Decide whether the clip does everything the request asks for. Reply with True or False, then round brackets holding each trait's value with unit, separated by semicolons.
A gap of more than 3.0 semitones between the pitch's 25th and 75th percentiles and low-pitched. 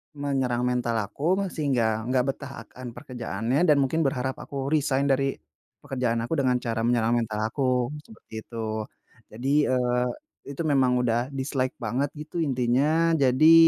False (2.7 semitones; 130 Hz)